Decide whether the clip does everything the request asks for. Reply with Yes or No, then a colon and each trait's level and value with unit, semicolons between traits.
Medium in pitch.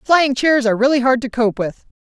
No: very high, 255 Hz